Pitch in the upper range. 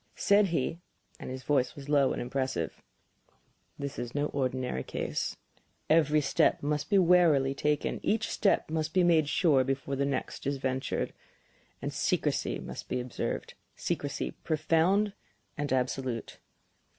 No: medium, 145 Hz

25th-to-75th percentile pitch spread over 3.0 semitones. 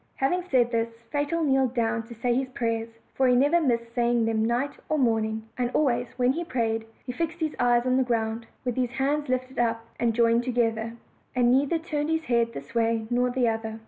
No: narrow, 2.6 semitones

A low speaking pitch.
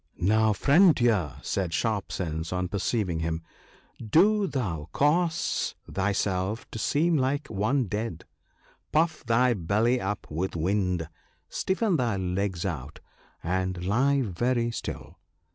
Yes: low, 105 Hz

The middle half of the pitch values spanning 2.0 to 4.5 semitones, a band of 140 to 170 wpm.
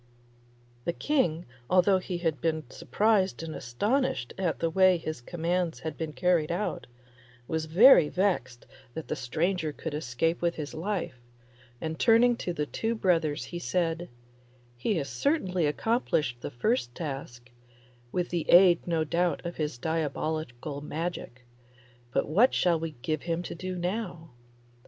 Yes: average, 3.1 semitones; average, 150 wpm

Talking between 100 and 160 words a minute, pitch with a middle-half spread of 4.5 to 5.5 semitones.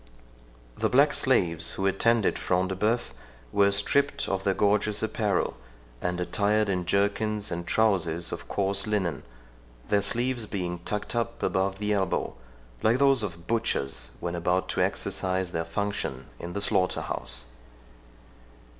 No: average, 145 wpm; average, 3.1 semitones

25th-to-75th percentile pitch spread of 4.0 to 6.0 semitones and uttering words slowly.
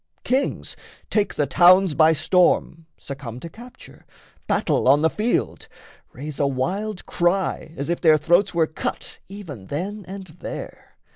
No: average, 4.8 semitones; average, 145 wpm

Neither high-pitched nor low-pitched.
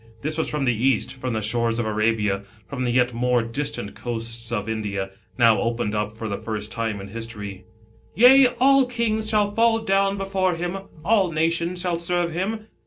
No: low, 125 Hz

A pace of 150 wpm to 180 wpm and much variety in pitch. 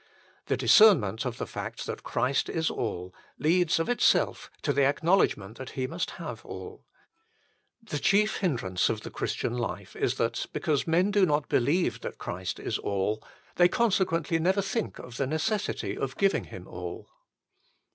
Yes: average, 165 wpm; wide, 8.1 semitones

